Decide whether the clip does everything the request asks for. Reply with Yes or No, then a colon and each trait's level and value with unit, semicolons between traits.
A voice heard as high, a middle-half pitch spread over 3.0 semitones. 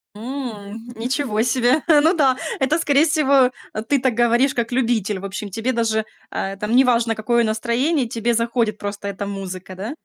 Yes: high, 235 Hz; average, 3.6 semitones